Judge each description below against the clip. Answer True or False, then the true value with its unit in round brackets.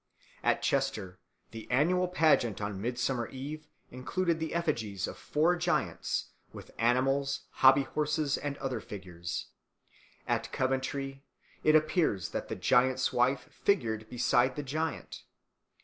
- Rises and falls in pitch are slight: False (4.4 semitones)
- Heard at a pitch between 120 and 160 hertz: True (135 Hz)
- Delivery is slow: True (125 wpm)